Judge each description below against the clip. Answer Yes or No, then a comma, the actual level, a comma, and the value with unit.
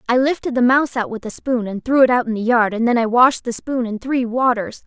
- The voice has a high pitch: Yes, high, 245 Hz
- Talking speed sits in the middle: No, fast, 295 wpm